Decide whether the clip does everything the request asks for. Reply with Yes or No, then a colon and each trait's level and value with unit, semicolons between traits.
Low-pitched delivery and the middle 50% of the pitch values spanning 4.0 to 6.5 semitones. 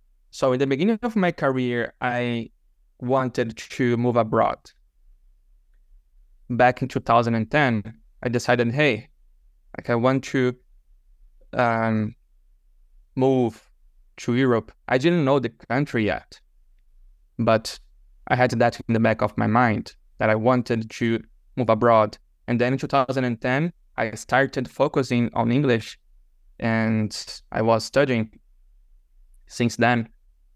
No: low, 115 Hz; average, 3.3 semitones